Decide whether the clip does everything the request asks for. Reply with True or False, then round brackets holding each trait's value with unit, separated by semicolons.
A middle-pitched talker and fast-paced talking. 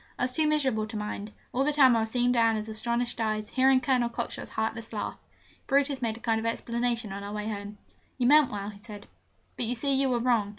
False (235 Hz; 230 wpm)